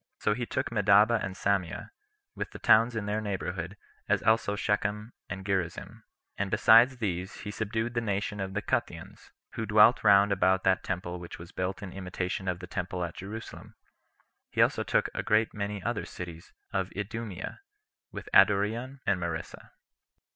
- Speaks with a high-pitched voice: No, low, 100 Hz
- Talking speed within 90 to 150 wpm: No, average, 170 wpm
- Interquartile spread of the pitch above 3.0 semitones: No, average, 2.7 semitones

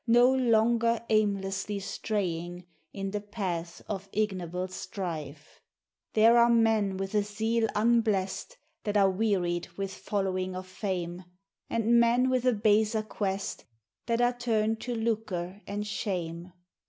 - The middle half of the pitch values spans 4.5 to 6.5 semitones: No, average, 3.3 semitones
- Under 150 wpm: Yes, slow, 135 wpm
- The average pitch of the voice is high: Yes, high, 205 Hz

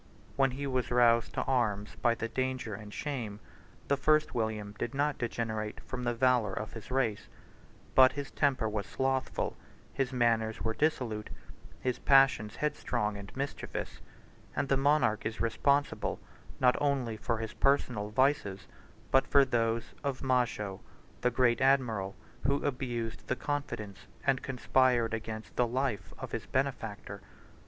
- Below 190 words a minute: Yes, average, 145 wpm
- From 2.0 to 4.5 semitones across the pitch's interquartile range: Yes, average, 3.5 semitones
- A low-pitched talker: Yes, low, 125 Hz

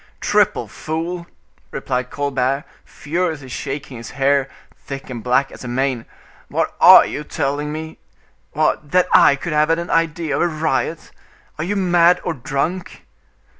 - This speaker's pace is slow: No, average, 155 wpm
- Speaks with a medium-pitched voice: Yes, medium, 150 Hz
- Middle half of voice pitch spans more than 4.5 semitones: No, average, 3.6 semitones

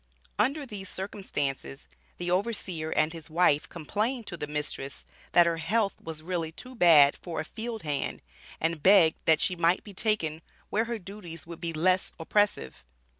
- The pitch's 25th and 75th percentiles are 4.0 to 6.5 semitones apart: Yes, average, 4.5 semitones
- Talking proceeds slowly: No, average, 170 wpm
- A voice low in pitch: No, medium, 175 Hz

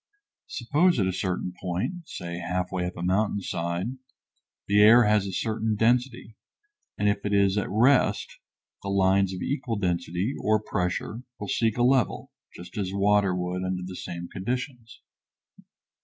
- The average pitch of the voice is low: Yes, low, 100 Hz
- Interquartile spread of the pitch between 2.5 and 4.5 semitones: Yes, average, 3.8 semitones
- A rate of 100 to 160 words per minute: Yes, average, 155 wpm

